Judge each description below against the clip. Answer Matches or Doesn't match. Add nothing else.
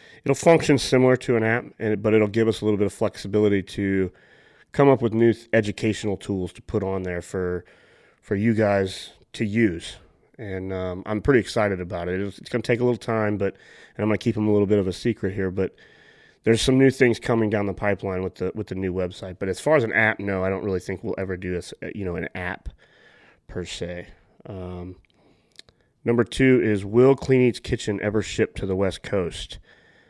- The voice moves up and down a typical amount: Matches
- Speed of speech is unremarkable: Doesn't match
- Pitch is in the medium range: Doesn't match